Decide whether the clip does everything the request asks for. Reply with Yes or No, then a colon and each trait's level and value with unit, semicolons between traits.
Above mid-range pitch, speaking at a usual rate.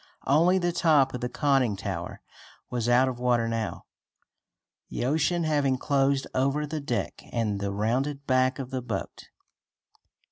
No: low, 130 Hz; average, 150 wpm